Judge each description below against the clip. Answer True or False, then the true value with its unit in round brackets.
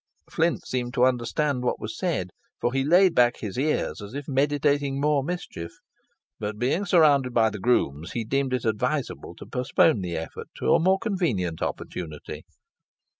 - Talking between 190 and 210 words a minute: False (170 wpm)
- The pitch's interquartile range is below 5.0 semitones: False (5.3 semitones)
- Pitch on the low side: True (130 Hz)